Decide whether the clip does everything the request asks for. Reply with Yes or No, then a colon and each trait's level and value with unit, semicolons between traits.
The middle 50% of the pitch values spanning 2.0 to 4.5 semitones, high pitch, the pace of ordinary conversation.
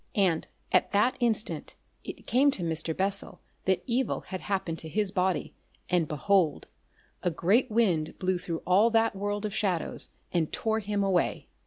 Yes: average, 3.5 semitones; high, 195 Hz; average, 165 wpm